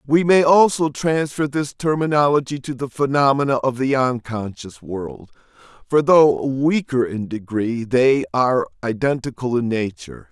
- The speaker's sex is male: Yes, male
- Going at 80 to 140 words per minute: Yes, slow, 135 wpm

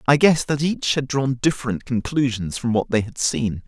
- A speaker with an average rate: No, fast, 210 wpm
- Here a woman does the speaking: No, male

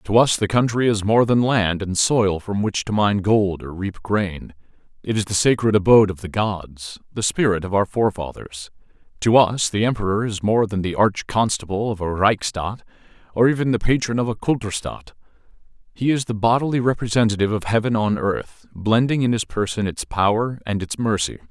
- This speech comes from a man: Yes, male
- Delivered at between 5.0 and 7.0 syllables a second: Yes, 5.2 syllables/s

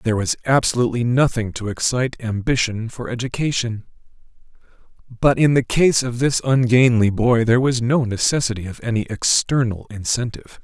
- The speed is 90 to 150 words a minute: Yes, average, 140 wpm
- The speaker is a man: Yes, male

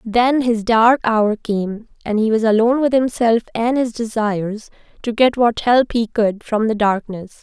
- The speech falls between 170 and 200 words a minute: Yes, average, 185 wpm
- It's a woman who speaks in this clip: Yes, female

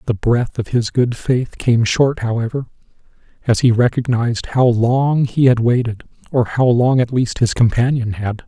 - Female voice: No, male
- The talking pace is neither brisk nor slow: Yes, average, 175 wpm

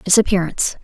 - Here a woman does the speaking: Yes, female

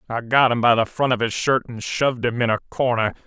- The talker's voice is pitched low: Yes, low, 120 Hz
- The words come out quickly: Yes, fast, 275 wpm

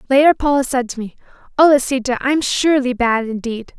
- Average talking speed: Yes, average, 175 wpm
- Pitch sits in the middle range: No, very high, 260 Hz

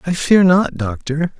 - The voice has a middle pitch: Yes, medium, 165 Hz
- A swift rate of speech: No, average, 175 wpm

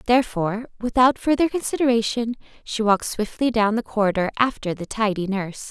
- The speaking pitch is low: No, high, 225 Hz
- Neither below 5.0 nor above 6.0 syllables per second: Yes, 5.9 syllables/s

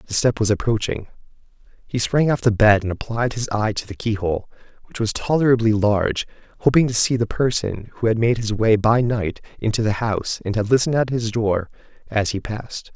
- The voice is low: Yes, low, 110 Hz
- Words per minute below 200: No, fast, 205 wpm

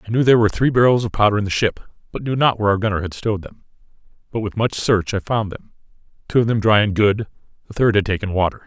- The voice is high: No, low, 105 Hz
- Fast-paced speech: Yes, fast, 265 wpm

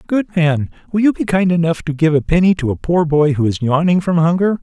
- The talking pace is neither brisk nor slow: No, fast, 260 wpm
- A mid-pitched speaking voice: Yes, medium, 165 Hz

